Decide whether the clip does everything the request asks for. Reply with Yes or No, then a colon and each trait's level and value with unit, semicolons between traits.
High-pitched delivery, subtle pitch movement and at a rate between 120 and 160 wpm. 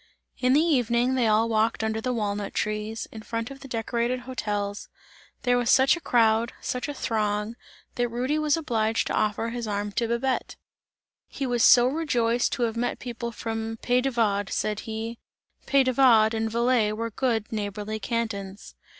No: high, 230 Hz; narrow, 2.3 semitones; average, 180 wpm